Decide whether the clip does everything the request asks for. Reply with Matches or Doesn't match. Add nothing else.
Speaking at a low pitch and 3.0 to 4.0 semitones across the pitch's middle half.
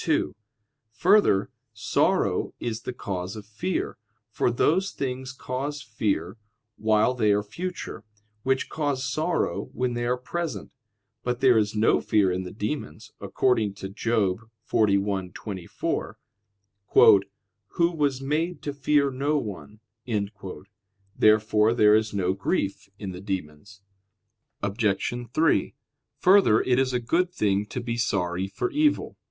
Doesn't match